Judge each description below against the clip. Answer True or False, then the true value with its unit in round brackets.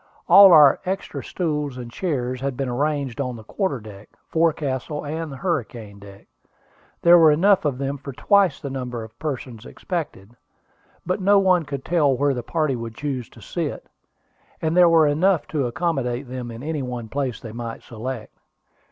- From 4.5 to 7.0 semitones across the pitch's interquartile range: True (4.9 semitones)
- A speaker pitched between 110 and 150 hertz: True (140 Hz)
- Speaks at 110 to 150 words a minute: False (175 wpm)